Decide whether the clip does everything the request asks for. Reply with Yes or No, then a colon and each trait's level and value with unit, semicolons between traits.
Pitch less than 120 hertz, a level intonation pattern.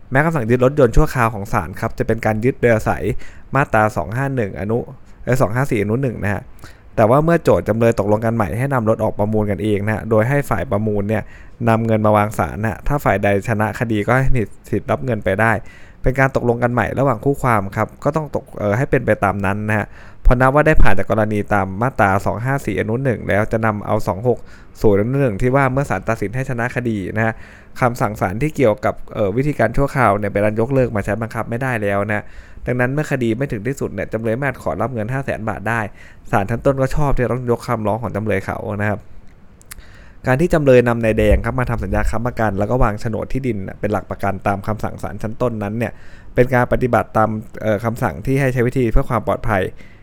No: low, 110 Hz; average, 3.4 semitones